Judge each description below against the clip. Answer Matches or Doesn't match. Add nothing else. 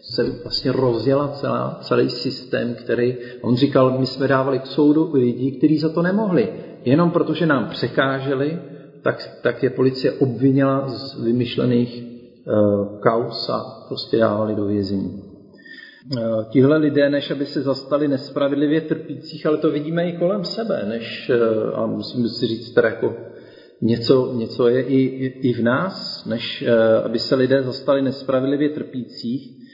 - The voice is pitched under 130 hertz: Doesn't match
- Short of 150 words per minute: Doesn't match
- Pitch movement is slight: Doesn't match